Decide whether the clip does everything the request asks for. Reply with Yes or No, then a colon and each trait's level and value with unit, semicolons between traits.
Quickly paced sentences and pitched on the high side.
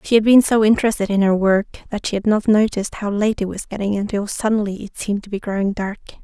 Yes: fast, 250 wpm; high, 205 Hz